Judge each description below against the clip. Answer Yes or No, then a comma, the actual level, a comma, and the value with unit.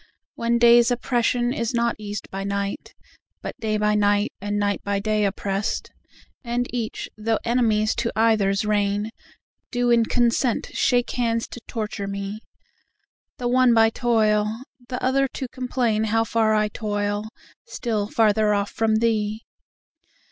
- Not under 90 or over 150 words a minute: Yes, average, 145 wpm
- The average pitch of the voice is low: No, high, 220 Hz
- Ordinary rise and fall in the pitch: No, narrow, 2.3 semitones